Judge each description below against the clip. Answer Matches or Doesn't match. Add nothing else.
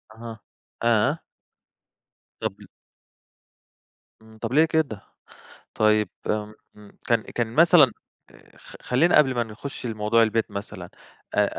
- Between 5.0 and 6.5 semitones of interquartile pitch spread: Doesn't match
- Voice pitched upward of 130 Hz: Doesn't match